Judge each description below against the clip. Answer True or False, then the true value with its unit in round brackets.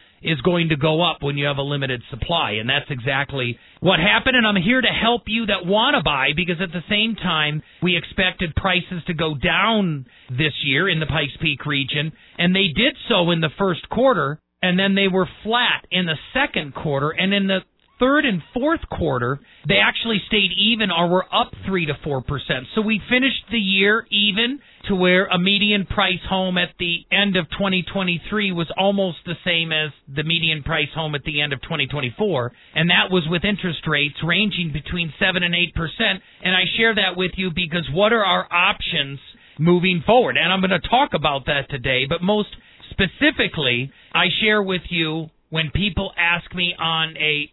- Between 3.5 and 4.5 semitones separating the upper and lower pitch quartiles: True (4.2 semitones)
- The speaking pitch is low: False (175 Hz)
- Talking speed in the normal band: True (195 wpm)